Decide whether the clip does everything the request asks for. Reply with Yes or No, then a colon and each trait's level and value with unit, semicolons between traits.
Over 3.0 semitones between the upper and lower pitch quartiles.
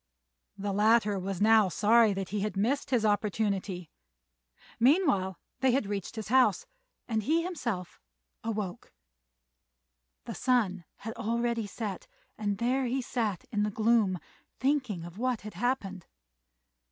Yes: average, 3.5 semitones